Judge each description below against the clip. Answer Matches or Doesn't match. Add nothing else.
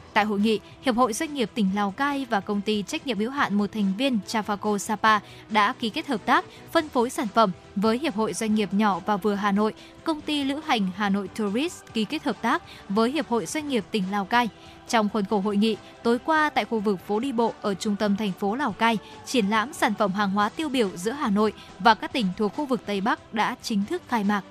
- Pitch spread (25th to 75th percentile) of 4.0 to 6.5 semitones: Doesn't match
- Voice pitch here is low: Doesn't match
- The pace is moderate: Doesn't match